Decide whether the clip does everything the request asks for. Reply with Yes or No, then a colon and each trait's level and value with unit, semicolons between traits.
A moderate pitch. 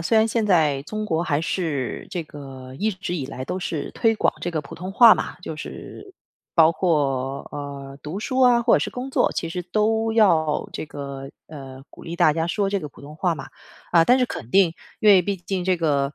Yes: medium, 165 Hz